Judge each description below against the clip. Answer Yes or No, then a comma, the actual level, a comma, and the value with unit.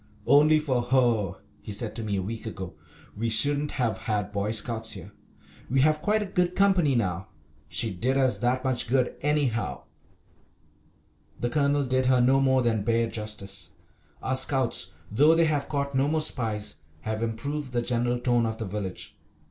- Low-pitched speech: Yes, low, 120 Hz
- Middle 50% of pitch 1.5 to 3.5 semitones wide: No, average, 4.4 semitones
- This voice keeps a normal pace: Yes, average, 175 wpm